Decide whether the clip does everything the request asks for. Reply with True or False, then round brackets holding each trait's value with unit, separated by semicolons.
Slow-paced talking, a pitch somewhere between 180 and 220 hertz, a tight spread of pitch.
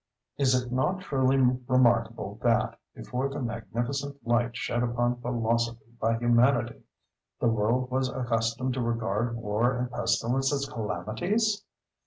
False (130 wpm; 120 Hz; 2.0 semitones)